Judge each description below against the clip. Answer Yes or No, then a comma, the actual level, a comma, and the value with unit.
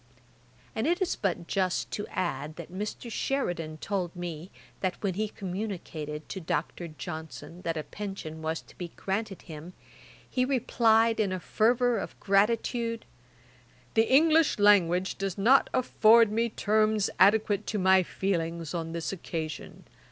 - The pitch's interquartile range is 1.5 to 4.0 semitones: No, average, 4.5 semitones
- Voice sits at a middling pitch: No, high, 195 Hz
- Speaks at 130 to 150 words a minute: Yes, average, 145 wpm